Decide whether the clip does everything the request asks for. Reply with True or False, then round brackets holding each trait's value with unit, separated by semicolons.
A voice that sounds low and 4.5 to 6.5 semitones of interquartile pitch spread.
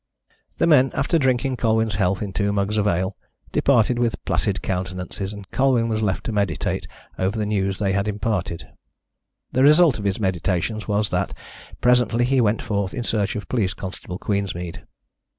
False (105 Hz; 3.6 semitones)